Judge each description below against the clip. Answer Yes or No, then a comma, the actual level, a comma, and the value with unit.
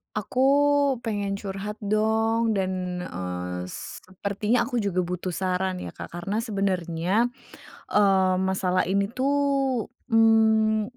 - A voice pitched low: No, high, 200 Hz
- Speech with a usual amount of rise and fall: Yes, average, 3.3 semitones